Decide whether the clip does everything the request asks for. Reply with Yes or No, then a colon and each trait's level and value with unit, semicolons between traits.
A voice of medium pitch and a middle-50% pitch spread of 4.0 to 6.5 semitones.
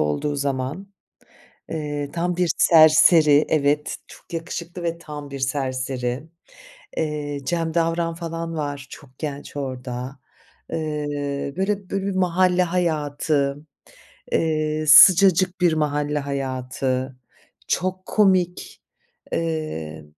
No: medium, 155 Hz; average, 3.3 semitones